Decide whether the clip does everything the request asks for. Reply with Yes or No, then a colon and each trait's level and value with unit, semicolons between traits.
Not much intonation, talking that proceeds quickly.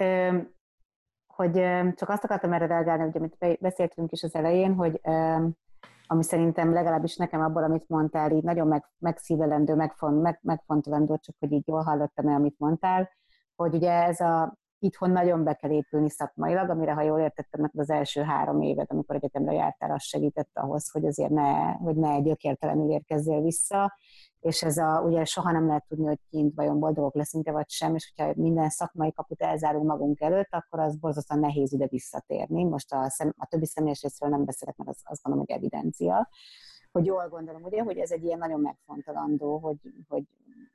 Yes: narrow, 2.1 semitones; fast, 185 wpm